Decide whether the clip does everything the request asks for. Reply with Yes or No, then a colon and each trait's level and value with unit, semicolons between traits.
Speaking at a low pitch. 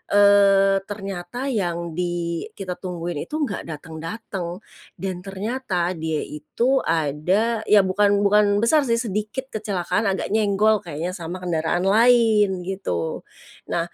No: high, 195 Hz